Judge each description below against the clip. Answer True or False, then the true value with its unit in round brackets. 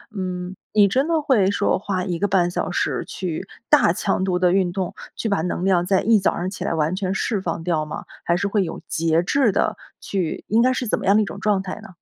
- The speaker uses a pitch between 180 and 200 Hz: True (190 Hz)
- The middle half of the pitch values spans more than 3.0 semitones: False (2.4 semitones)